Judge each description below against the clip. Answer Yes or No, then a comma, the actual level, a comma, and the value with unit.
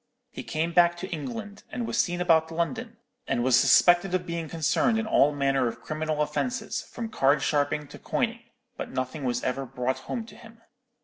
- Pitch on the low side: No, medium, 165 Hz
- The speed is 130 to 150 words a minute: No, average, 190 wpm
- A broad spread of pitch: Yes, wide, 6.5 semitones